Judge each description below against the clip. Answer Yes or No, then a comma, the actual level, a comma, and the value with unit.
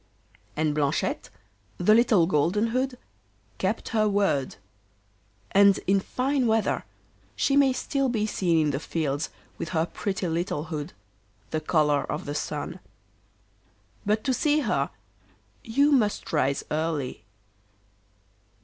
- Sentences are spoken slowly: Yes, slow, 125 wpm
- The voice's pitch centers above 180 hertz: Yes, high, 190 Hz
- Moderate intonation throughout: No, wide, 6.8 semitones